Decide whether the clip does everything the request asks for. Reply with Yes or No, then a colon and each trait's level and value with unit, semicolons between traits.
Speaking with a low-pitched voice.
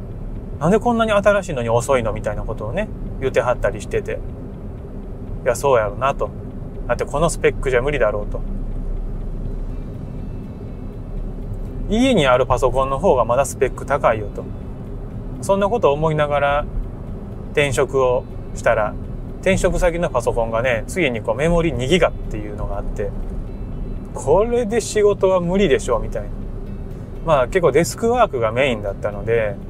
Yes: low, 125 Hz